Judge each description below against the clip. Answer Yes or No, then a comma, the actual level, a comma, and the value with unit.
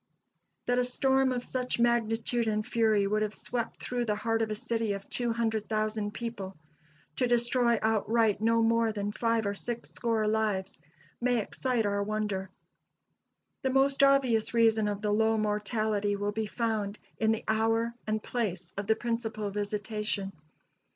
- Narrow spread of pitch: Yes, narrow, 2.0 semitones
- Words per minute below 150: No, average, 155 wpm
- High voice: Yes, high, 220 Hz